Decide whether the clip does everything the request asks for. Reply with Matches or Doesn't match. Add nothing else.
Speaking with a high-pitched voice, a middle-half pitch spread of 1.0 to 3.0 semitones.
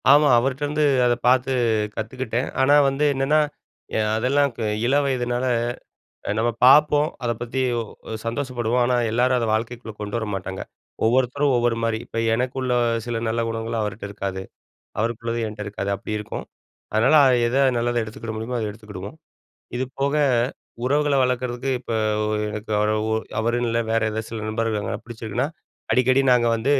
Doesn't match